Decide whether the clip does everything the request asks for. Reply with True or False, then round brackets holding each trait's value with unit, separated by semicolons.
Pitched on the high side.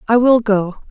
True (220 Hz)